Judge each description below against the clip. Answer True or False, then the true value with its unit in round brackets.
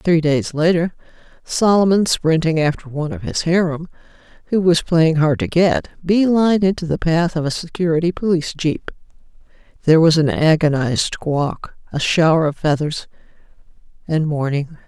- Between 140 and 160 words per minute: True (150 wpm)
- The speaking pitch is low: False (160 Hz)